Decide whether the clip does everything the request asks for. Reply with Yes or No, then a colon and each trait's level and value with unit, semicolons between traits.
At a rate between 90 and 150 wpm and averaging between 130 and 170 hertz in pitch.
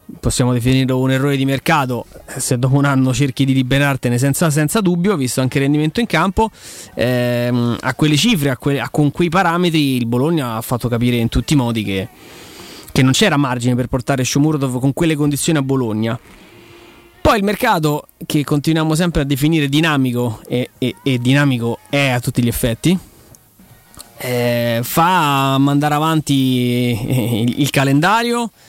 No: average, 165 wpm; low, 135 Hz